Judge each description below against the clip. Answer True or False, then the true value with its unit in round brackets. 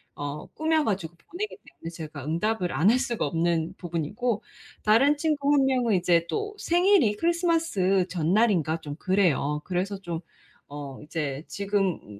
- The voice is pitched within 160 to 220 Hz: True (190 Hz)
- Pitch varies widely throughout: True (8.0 semitones)